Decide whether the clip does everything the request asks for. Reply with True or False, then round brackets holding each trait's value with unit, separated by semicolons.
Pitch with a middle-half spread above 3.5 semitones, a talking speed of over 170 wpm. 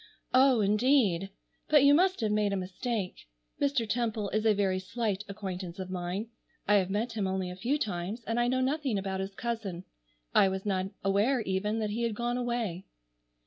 True (3.9 semitones; 190 wpm)